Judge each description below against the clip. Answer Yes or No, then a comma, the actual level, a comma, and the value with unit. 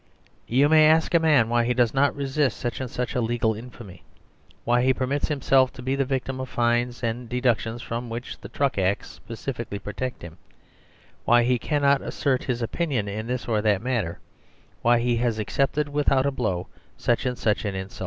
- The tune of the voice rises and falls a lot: No, average, 2.7 semitones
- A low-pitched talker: Yes, low, 125 Hz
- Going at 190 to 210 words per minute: Yes, average, 195 wpm